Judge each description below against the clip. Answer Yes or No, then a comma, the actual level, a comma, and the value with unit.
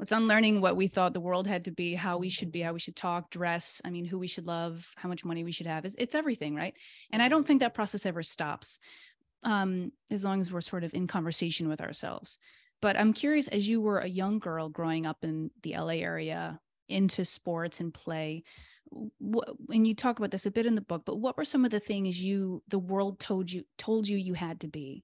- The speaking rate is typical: No, fast, 245 wpm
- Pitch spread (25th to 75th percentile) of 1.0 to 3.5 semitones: No, average, 3.9 semitones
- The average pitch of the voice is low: No, medium, 185 Hz